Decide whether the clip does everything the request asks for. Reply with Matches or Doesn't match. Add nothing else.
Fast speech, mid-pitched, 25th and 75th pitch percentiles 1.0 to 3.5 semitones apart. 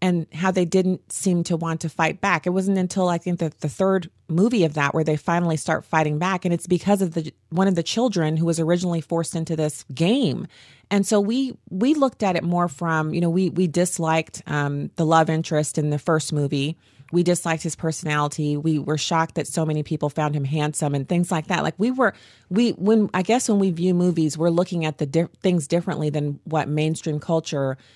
Matches